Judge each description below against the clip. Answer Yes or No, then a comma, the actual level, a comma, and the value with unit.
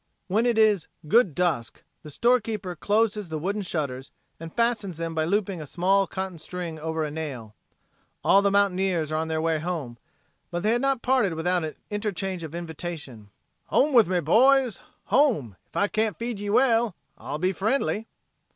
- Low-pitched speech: No, medium, 185 Hz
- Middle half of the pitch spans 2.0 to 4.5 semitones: No, average, 5.2 semitones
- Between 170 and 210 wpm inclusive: Yes, average, 180 wpm